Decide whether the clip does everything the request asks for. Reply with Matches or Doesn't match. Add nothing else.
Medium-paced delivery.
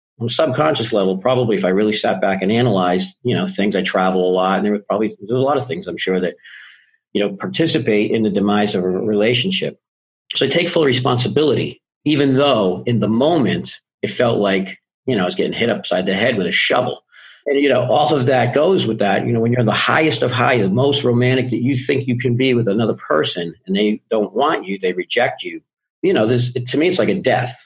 Doesn't match